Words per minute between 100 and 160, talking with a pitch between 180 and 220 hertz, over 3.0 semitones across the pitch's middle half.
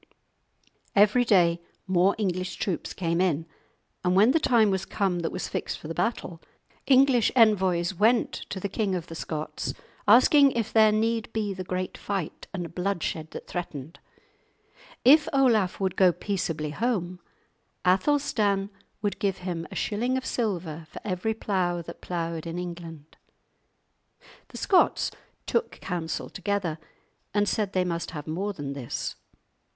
Yes: average, 150 wpm; high, 190 Hz; average, 4.1 semitones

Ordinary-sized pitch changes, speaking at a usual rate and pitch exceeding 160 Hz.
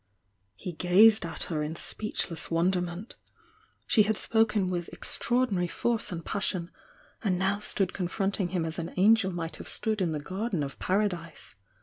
Yes: average, 3.6 semitones; average, 155 wpm; medium, 185 Hz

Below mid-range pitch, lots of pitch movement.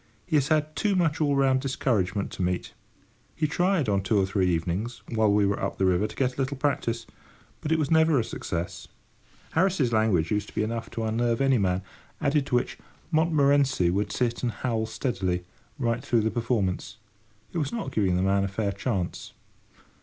Yes: low, 115 Hz; wide, 6.1 semitones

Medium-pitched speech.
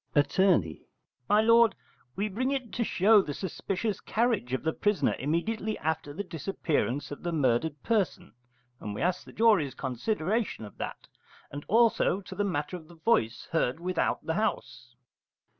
Yes: medium, 180 Hz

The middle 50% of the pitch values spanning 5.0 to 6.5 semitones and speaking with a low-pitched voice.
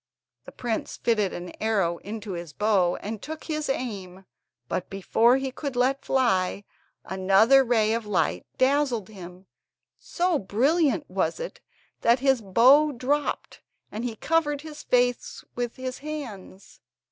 No: wide, 5.6 semitones; high, 235 Hz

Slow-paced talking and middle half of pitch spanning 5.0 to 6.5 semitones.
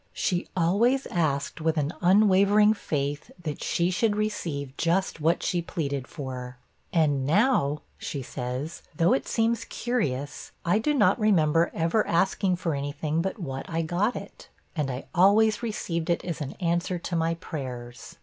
No: average, 160 wpm; wide, 5.4 semitones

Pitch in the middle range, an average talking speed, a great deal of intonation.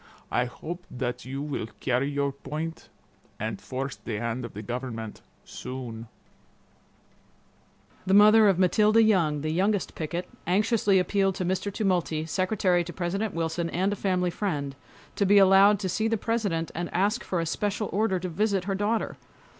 Yes: medium, 180 Hz; average, 165 wpm; wide, 6.0 semitones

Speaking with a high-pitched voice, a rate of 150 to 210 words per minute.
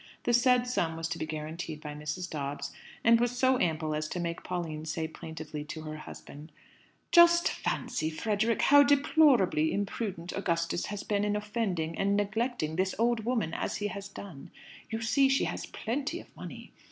Yes: high, 195 Hz; average, 175 wpm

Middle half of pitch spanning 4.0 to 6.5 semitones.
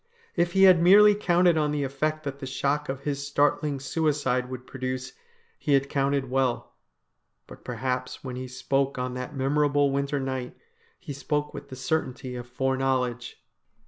No: narrow, 2.5 semitones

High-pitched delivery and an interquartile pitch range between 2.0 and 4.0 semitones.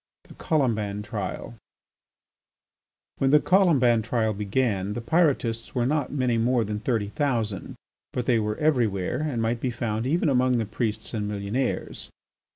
No: low, 115 Hz; average, 3.6 semitones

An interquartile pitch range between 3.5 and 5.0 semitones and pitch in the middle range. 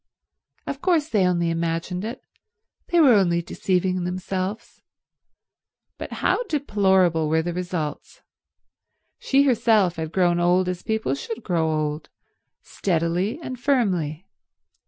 Yes: average, 4.5 semitones; medium, 180 Hz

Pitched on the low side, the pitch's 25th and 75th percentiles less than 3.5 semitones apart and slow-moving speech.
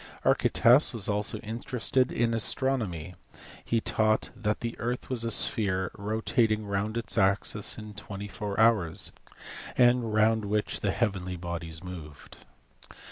Yes: low, 105 Hz; average, 2.9 semitones; slow, 130 wpm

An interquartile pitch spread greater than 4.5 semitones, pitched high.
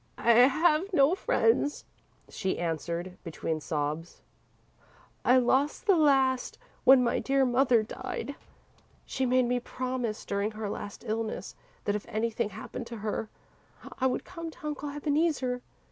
Yes: average, 4.9 semitones; very high, 250 Hz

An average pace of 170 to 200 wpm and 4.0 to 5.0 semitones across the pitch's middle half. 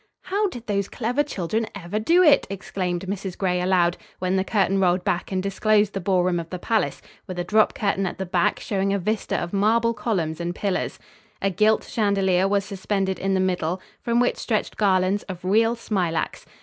No: average, 195 wpm; average, 2.7 semitones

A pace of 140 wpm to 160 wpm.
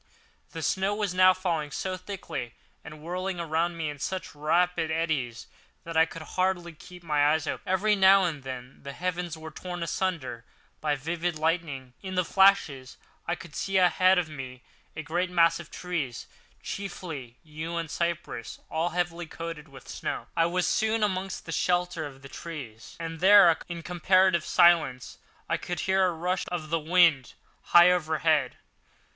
No: average, 170 wpm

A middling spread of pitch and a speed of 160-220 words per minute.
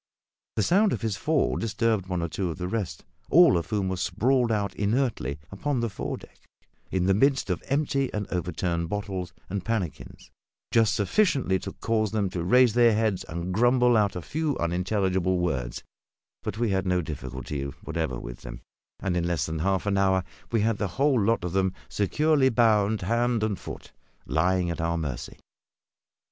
Yes: average, 4.7 semitones; average, 180 wpm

